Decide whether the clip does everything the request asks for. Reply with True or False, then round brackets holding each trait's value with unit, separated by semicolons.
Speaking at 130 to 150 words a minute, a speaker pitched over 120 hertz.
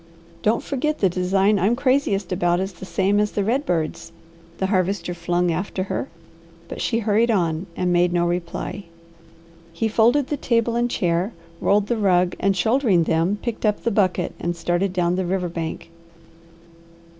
False (175 wpm; 190 Hz)